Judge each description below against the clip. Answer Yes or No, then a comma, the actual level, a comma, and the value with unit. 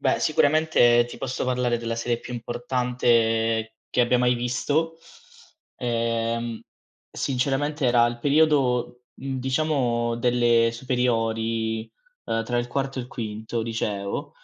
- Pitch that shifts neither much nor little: No, narrow, 1.9 semitones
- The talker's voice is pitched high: No, low, 120 Hz